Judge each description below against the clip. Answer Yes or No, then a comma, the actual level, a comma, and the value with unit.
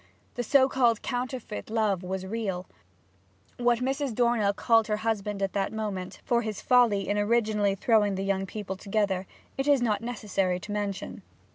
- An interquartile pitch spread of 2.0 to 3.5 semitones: Yes, average, 3.2 semitones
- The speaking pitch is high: Yes, high, 210 Hz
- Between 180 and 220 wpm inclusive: No, average, 165 wpm